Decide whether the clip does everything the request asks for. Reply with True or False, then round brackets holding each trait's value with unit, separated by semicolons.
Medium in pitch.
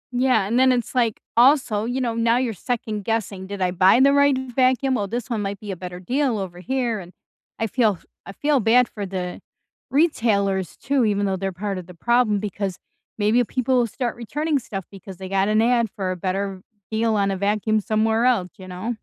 False (220 Hz)